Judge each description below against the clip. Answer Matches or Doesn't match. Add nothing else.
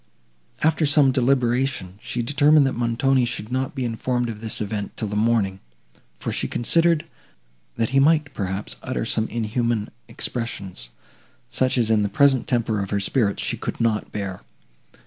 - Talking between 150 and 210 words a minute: Matches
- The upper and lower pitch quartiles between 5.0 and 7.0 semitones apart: Doesn't match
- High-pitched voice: Doesn't match